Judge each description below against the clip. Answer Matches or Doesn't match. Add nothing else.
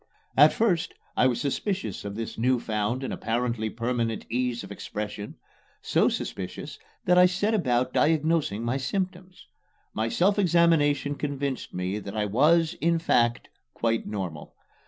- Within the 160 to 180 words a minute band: Doesn't match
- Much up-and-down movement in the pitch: Matches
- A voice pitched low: Matches